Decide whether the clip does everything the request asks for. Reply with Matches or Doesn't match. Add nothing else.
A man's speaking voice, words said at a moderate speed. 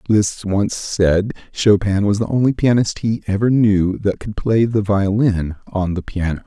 Matches